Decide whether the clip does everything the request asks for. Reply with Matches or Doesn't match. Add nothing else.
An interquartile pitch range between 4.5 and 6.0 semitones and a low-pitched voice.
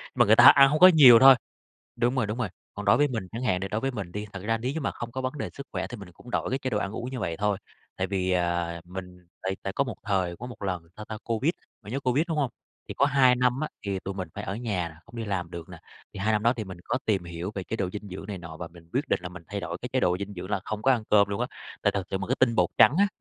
Matches